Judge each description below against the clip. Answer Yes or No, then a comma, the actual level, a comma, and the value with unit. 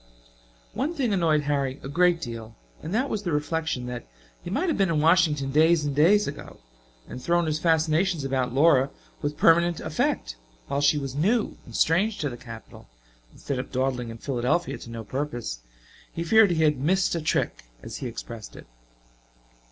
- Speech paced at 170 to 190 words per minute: Yes, average, 185 wpm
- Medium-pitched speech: Yes, medium, 150 Hz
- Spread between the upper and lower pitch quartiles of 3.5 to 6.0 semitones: Yes, average, 4.8 semitones